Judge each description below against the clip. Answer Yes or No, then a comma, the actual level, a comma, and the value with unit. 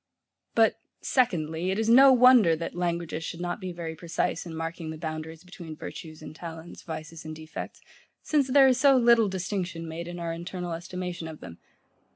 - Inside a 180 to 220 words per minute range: Yes, average, 185 wpm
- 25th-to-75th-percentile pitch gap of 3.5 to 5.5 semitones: No, average, 3.1 semitones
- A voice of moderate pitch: Yes, medium, 170 Hz